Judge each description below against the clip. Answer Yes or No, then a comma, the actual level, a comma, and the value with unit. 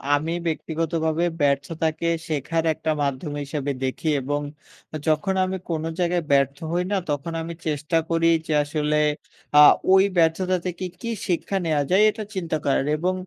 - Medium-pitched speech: Yes, medium, 160 Hz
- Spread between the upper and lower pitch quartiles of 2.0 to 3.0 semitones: Yes, average, 2.7 semitones